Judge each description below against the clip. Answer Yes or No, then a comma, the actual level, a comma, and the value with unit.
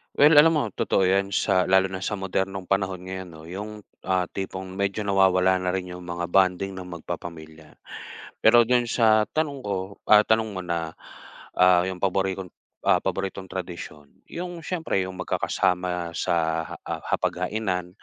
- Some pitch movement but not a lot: No, narrow, 1.9 semitones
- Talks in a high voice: No, very low, 95 Hz